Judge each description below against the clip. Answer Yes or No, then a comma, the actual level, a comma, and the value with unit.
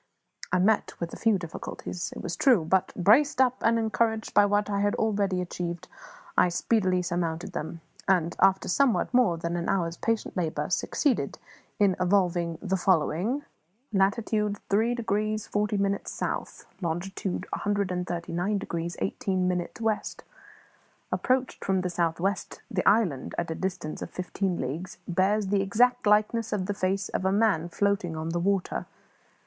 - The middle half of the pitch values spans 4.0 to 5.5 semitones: No, average, 3.3 semitones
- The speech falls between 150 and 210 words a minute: Yes, average, 155 wpm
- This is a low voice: No, high, 195 Hz